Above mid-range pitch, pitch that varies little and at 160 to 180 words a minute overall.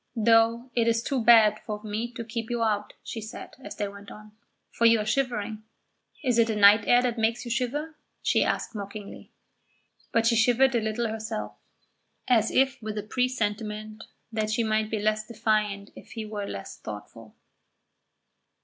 Yes: high, 220 Hz; narrow, 1.9 semitones; average, 175 wpm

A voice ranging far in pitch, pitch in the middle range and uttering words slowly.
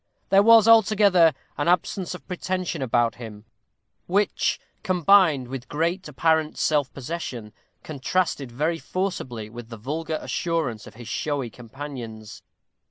Yes: wide, 6.7 semitones; medium, 155 Hz; slow, 125 wpm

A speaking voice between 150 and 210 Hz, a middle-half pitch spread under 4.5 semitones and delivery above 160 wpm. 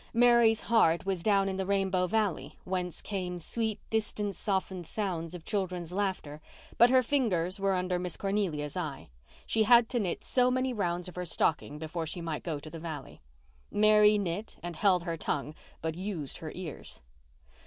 Yes: medium, 185 Hz; average, 3.9 semitones; average, 175 wpm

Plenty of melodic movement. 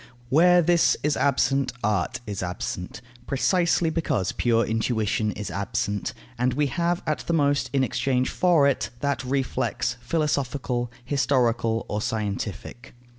No: average, 4.4 semitones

